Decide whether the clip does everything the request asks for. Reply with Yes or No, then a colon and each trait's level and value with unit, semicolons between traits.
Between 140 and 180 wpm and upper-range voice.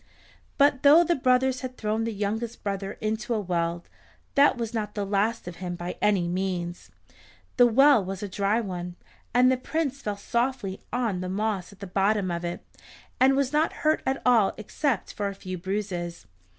No: average, 190 wpm; high, 210 Hz